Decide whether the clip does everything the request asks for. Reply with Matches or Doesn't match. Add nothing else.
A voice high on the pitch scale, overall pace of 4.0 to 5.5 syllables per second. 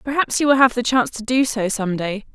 Doesn't match